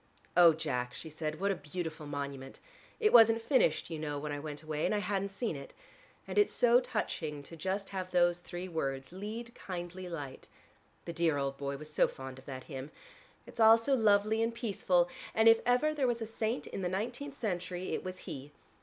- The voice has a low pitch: No, medium, 180 Hz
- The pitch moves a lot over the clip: Yes, wide, 6.7 semitones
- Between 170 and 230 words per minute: Yes, fast, 205 wpm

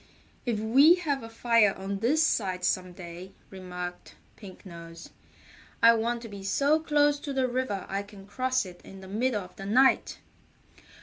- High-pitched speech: Yes, high, 210 Hz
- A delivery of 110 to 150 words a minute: No, average, 175 wpm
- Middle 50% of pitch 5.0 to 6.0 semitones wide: Yes, average, 5.3 semitones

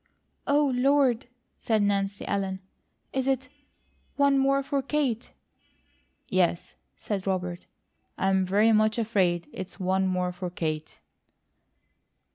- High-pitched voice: Yes, high, 200 Hz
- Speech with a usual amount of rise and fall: No, wide, 5.9 semitones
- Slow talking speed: Yes, slow, 115 wpm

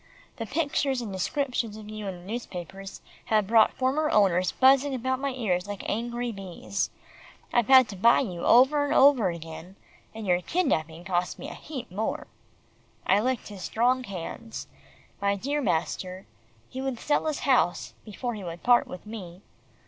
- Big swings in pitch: Yes, wide, 5.7 semitones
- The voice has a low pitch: No, high, 220 Hz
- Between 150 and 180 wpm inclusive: Yes, average, 170 wpm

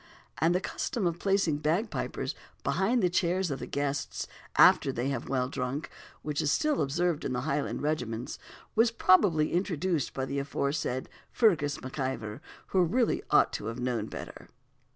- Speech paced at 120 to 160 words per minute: Yes, average, 155 wpm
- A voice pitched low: No, medium, 150 Hz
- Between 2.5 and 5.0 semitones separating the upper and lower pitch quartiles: No, wide, 5.5 semitones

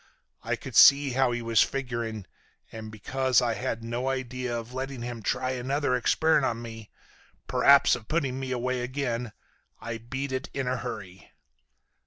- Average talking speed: Yes, average, 165 wpm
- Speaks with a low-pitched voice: Yes, low, 125 Hz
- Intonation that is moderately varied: No, narrow, 2.3 semitones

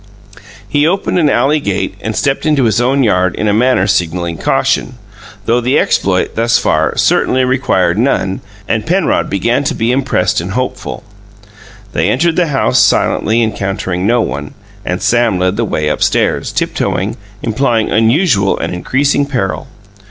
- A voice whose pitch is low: Yes, low, 115 Hz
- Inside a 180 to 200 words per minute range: No, average, 155 wpm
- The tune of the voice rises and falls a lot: Yes, wide, 5.8 semitones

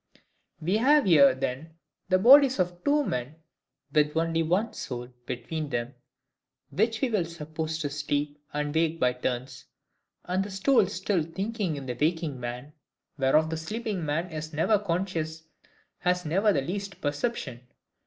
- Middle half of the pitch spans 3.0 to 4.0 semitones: No, average, 5.0 semitones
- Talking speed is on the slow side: No, average, 155 wpm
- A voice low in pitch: No, medium, 160 Hz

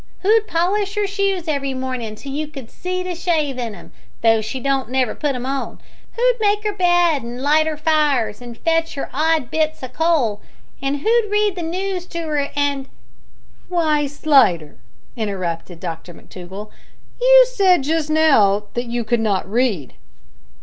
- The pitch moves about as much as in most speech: No, wide, 6.5 semitones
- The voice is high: Yes, very high, 290 Hz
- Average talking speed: Yes, average, 170 wpm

